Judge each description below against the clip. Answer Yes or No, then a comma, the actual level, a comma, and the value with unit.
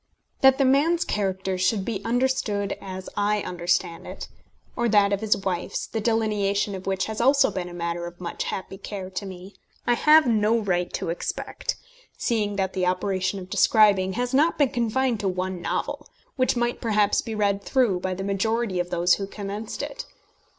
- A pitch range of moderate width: Yes, average, 3.7 semitones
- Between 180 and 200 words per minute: Yes, average, 190 wpm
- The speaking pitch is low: No, high, 200 Hz